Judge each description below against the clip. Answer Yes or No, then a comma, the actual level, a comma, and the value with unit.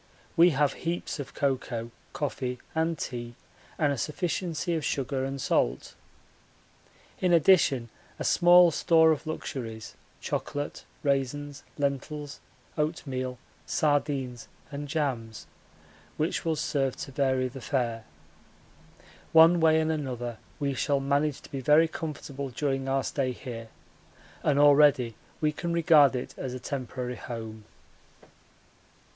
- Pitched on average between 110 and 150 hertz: Yes, medium, 140 Hz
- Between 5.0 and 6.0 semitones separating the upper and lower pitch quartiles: No, average, 3.3 semitones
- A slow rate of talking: Yes, slow, 125 wpm